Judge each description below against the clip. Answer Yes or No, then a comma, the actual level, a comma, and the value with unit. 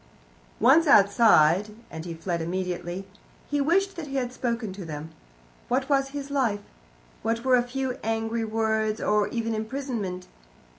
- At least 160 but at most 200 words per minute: No, average, 150 wpm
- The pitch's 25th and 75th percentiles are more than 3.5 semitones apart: Yes, wide, 5.4 semitones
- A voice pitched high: Yes, high, 225 Hz